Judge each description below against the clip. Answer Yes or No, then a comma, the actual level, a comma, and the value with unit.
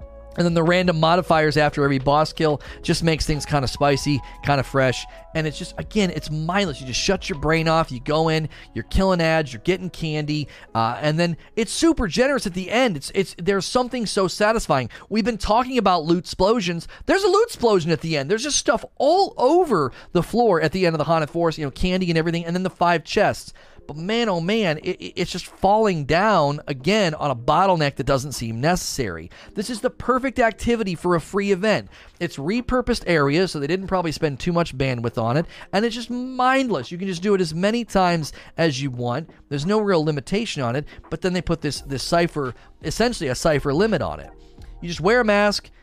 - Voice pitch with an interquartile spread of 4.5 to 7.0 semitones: Yes, wide, 5.5 semitones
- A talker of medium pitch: Yes, medium, 170 Hz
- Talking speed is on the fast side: Yes, fast, 220 wpm